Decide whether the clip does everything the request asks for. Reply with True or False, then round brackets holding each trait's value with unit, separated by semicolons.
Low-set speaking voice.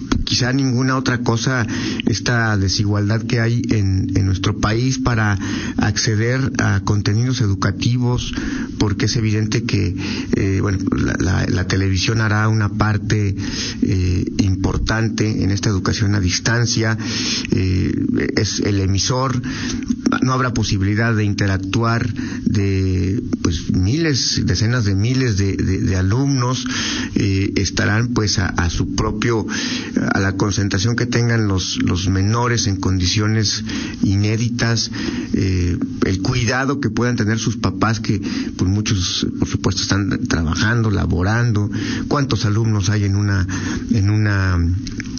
True (110 Hz)